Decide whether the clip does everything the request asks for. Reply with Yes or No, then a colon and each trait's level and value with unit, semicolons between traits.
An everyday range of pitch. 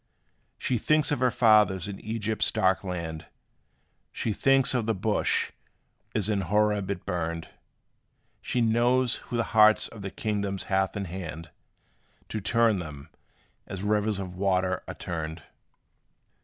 Yes: average, 3.3 semitones